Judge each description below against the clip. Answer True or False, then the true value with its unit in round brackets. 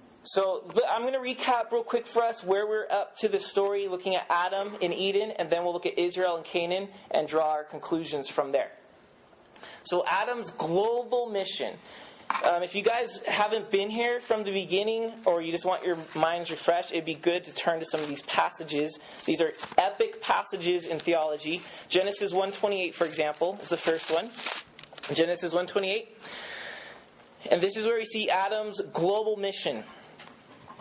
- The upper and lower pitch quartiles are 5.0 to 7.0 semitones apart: False (4.1 semitones)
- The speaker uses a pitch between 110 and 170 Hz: False (190 Hz)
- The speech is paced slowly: False (175 wpm)